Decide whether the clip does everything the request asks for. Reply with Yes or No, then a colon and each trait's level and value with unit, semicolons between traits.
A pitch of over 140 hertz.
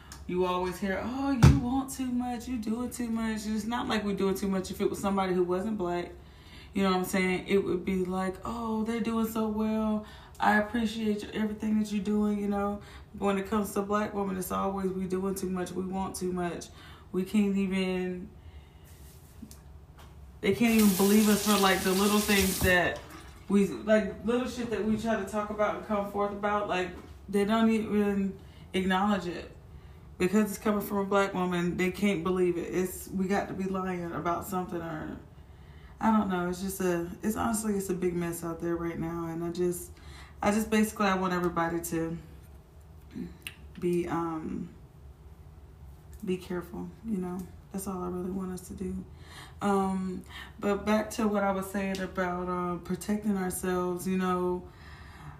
Yes: high, 190 Hz